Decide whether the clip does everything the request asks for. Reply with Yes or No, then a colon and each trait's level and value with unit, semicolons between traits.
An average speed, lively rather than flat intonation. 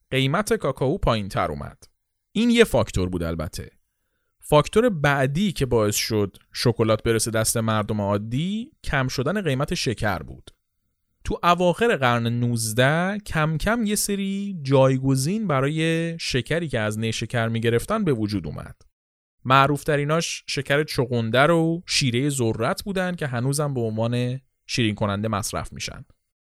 Yes: average, 135 wpm; wide, 6.7 semitones